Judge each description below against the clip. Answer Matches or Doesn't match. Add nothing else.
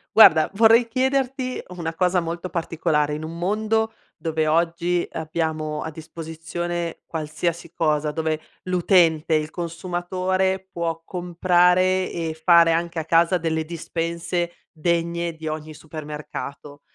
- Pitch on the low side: Doesn't match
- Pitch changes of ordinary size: Doesn't match